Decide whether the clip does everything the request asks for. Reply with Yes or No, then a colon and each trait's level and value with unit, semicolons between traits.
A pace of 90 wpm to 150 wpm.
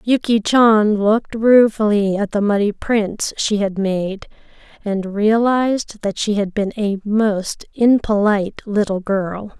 Yes: average, 140 wpm